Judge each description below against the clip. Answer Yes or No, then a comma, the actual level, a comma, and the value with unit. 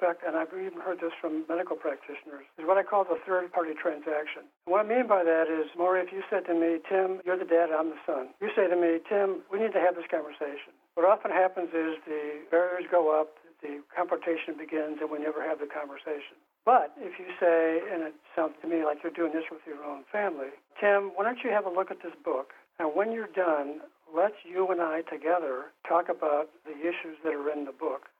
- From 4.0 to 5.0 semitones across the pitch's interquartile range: No, average, 3.0 semitones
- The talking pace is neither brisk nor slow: No, fast, 230 wpm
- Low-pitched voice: No, medium, 165 Hz